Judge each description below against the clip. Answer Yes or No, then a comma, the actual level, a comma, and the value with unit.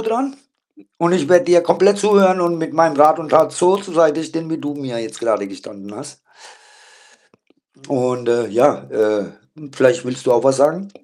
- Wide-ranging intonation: Yes, wide, 5.9 semitones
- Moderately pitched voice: Yes, medium, 155 Hz